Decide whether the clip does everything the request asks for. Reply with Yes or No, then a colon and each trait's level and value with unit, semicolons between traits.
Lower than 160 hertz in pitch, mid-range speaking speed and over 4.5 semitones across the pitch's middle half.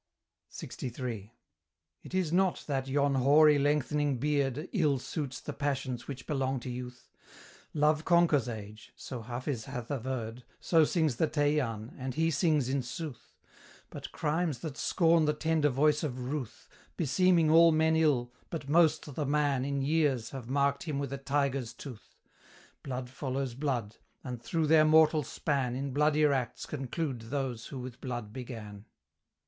No: medium, 140 Hz; average, 155 wpm; average, 3.3 semitones